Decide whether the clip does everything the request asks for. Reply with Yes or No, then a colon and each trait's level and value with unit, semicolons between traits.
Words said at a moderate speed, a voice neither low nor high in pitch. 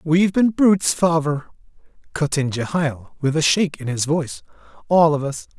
Yes: average, 170 wpm; medium, 155 Hz